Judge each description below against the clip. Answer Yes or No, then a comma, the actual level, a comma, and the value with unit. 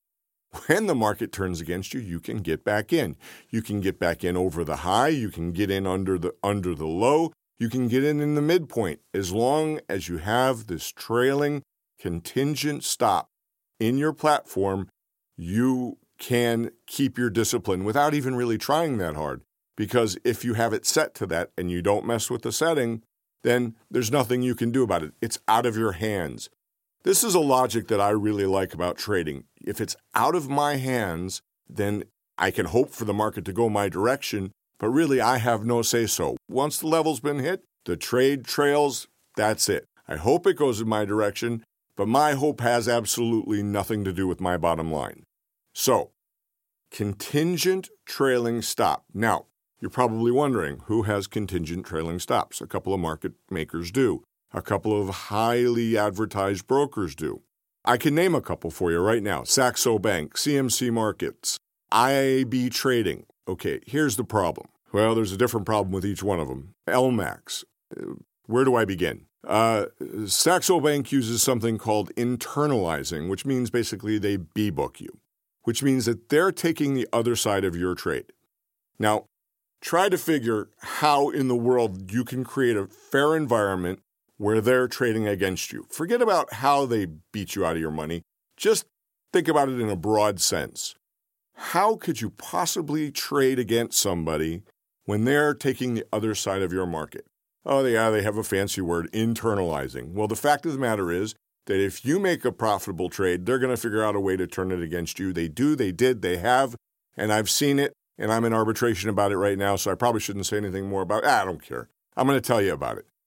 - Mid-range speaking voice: No, low, 110 Hz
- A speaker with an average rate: Yes, average, 190 wpm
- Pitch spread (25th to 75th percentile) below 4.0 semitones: No, average, 4.9 semitones